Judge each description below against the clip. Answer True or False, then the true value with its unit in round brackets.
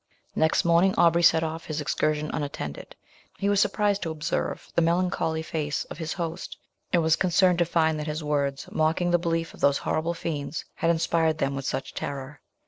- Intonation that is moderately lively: False (2.1 semitones)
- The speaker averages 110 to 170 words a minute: False (195 wpm)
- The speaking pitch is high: False (160 Hz)